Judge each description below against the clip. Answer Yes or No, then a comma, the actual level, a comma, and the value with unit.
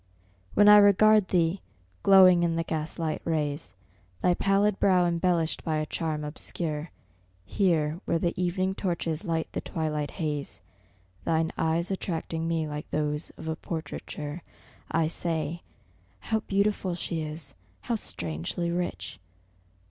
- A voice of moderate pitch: Yes, medium, 165 Hz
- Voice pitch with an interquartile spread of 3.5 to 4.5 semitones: No, average, 2.9 semitones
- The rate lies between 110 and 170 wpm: Yes, slow, 135 wpm